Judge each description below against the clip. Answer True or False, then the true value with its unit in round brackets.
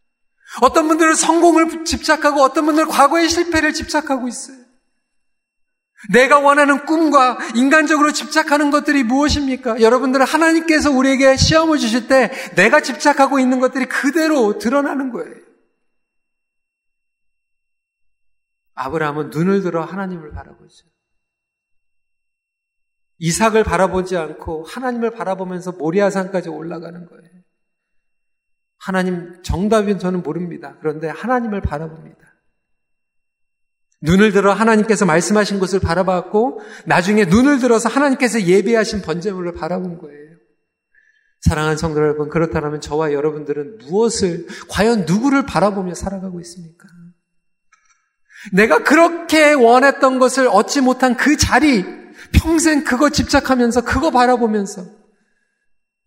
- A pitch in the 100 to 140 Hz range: False (225 Hz)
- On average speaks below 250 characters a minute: False (305 characters per minute)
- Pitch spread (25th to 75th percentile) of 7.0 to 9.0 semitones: True (7.7 semitones)